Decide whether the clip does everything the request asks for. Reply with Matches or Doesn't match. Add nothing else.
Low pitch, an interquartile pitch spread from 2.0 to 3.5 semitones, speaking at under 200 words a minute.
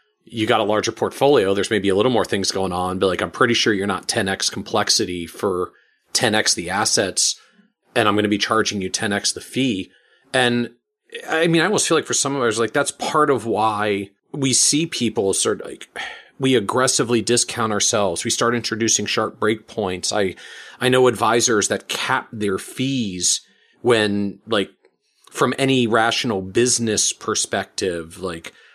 Doesn't match